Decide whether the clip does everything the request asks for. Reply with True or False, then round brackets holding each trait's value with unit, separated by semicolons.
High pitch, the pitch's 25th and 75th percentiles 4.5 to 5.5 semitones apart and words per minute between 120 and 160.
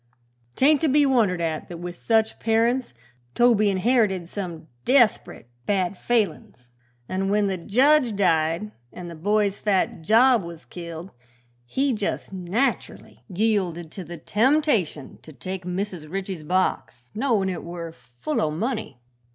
True (195 Hz; 4.9 semitones; 140 wpm)